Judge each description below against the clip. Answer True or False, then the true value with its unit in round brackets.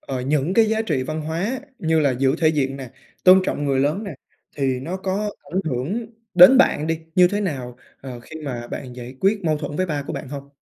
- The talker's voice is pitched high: False (155 Hz)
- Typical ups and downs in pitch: False (5.7 semitones)